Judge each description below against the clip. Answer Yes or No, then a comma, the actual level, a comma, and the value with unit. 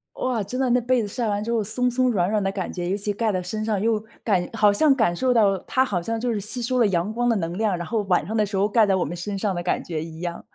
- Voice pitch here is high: Yes, high, 210 Hz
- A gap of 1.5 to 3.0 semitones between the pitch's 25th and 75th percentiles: No, average, 3.6 semitones